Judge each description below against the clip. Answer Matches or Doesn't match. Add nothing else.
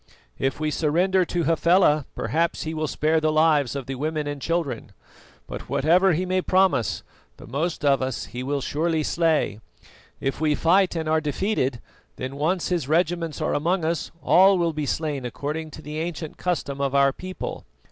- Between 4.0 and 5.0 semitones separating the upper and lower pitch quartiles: Doesn't match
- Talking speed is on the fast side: Doesn't match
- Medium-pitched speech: Matches